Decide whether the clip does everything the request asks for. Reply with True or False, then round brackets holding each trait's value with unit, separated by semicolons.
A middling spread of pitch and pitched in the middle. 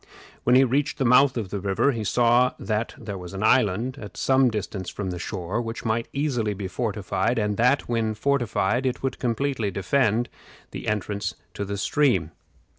False (3.9 semitones; 110 Hz)